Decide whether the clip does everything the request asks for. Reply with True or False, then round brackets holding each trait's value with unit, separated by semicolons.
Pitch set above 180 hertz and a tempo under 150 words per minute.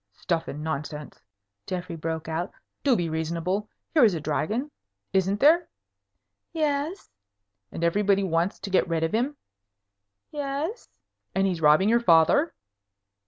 True (190 Hz; 135 wpm)